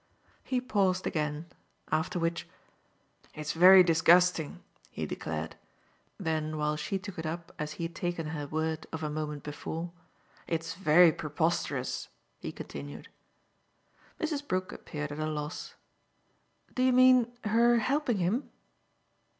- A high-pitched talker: No, medium, 165 Hz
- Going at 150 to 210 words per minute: No, slow, 135 wpm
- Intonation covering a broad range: No, average, 3.9 semitones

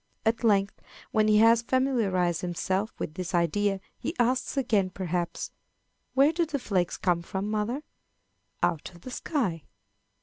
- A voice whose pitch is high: Yes, high, 205 Hz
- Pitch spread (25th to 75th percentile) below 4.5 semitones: No, average, 5.2 semitones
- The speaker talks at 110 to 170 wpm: Yes, average, 145 wpm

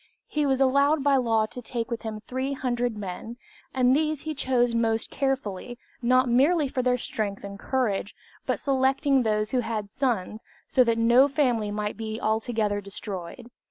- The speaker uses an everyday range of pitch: Yes, average, 3.5 semitones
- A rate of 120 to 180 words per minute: Yes, average, 165 wpm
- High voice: Yes, high, 240 Hz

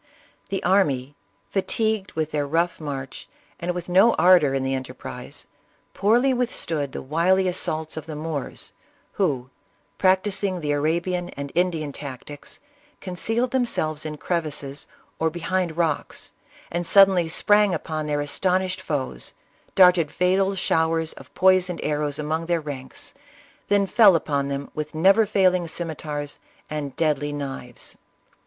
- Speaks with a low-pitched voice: No, medium, 165 Hz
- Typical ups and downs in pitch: Yes, average, 4.1 semitones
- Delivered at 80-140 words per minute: Yes, slow, 135 wpm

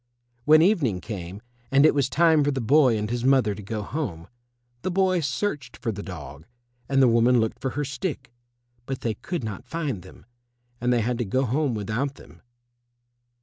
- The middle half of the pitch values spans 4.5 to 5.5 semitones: Yes, average, 5.2 semitones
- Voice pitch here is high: No, low, 125 Hz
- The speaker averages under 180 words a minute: No, average, 190 wpm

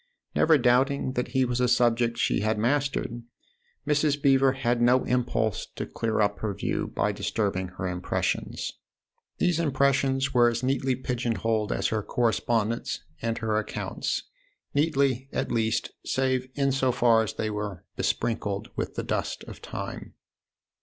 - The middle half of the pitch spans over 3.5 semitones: No, average, 3.0 semitones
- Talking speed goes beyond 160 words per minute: No, average, 155 wpm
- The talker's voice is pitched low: Yes, low, 120 Hz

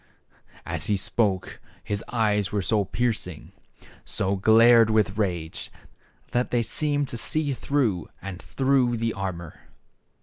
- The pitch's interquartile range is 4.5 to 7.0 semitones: No, average, 3.9 semitones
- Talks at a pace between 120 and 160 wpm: Yes, average, 140 wpm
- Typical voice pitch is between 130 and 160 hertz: No, low, 110 Hz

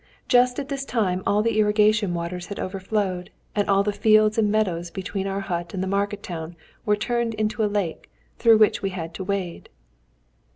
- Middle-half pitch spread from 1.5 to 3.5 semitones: Yes, narrow, 2.6 semitones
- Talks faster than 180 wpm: Yes, average, 195 wpm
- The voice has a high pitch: Yes, high, 205 Hz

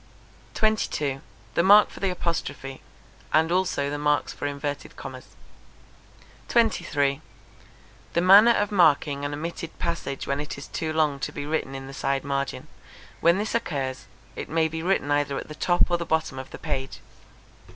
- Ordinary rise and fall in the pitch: Yes, average, 3.6 semitones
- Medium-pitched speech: Yes, medium, 150 Hz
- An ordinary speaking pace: Yes, average, 170 wpm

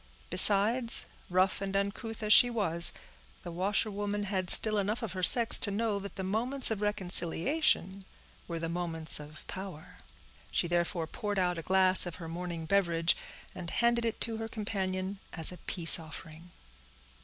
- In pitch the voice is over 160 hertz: Yes, high, 190 Hz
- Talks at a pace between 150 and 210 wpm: Yes, average, 165 wpm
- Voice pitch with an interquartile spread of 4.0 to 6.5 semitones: No, average, 3.4 semitones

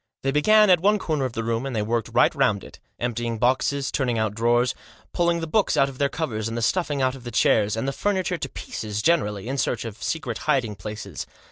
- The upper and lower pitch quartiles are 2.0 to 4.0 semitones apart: No, average, 5.1 semitones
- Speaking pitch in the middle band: No, low, 125 Hz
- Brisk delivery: Yes, fast, 235 wpm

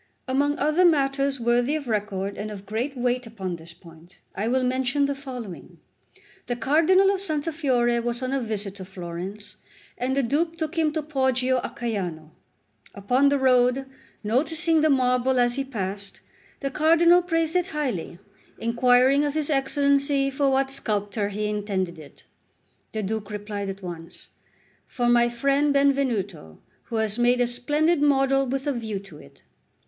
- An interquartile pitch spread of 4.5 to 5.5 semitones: Yes, average, 5.2 semitones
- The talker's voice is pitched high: Yes, very high, 250 Hz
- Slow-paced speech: No, average, 165 wpm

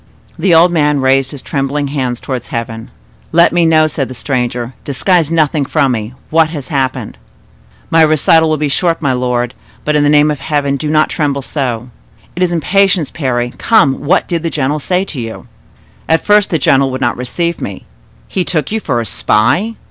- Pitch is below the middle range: No, medium, 145 Hz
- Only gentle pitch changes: No, average, 4.0 semitones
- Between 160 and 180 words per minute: No, average, 190 wpm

